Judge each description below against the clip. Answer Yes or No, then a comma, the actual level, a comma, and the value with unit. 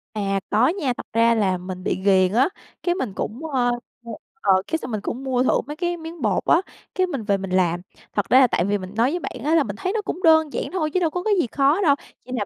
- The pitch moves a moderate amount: No, wide, 8.1 semitones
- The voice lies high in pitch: Yes, very high, 250 Hz